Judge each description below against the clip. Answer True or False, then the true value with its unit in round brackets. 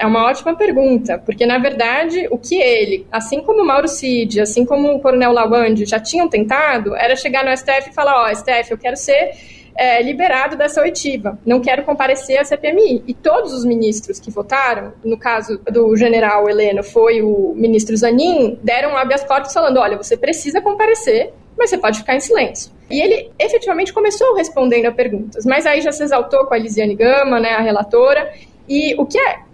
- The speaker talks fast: True (200 wpm)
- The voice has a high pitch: True (260 Hz)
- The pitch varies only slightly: False (4.5 semitones)